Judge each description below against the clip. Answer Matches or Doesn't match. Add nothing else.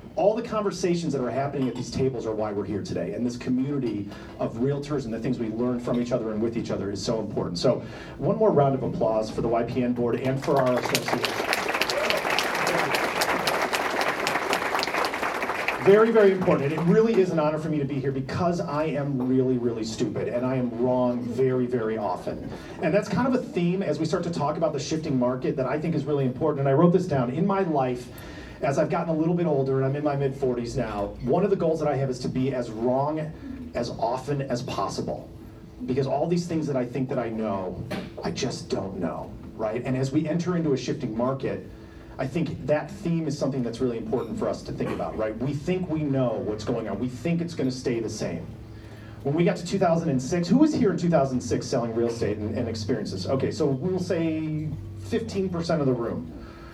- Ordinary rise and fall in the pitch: Matches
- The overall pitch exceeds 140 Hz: Doesn't match